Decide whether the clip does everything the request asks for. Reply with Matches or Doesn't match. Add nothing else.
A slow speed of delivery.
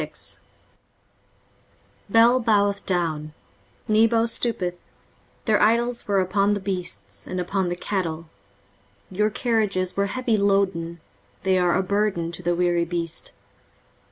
Matches